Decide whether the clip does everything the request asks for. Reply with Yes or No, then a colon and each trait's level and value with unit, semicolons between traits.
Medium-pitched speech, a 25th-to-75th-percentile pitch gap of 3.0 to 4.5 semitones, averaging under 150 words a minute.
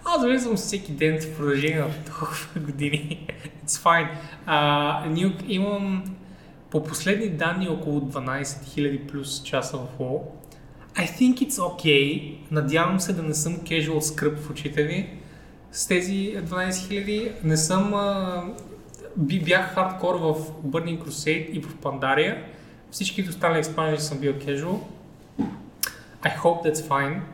Yes: medium, 160 Hz; average, 3.7 semitones; average, 140 wpm